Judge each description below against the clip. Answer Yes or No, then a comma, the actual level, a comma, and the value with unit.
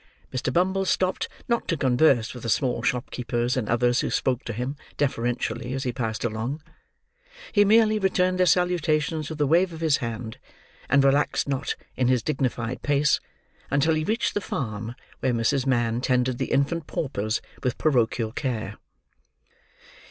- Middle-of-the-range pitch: No, low, 130 Hz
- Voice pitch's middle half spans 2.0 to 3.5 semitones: No, average, 4.6 semitones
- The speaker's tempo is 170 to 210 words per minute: No, average, 160 wpm